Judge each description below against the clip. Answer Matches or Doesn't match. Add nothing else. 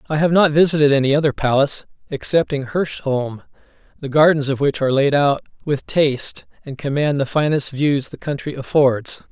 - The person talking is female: Doesn't match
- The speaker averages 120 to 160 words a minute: Doesn't match